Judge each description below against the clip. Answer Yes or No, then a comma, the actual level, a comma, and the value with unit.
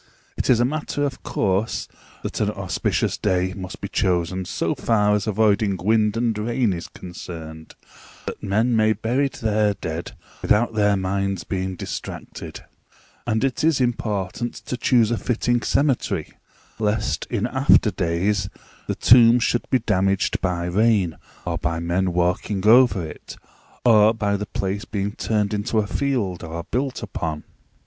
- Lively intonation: No, average, 3.8 semitones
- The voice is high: No, low, 105 Hz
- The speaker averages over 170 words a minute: No, average, 155 wpm